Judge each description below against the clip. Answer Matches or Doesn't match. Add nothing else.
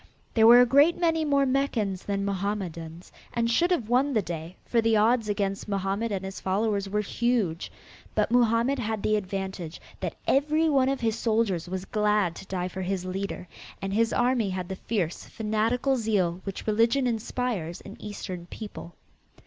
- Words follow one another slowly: Doesn't match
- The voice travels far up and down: Doesn't match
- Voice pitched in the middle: Doesn't match